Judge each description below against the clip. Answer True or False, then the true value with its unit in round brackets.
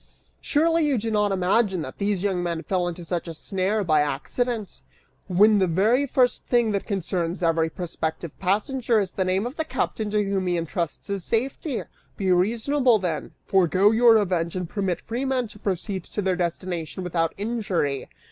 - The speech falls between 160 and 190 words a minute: True (180 wpm)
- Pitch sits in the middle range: False (195 Hz)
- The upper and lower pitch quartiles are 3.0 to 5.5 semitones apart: True (4.1 semitones)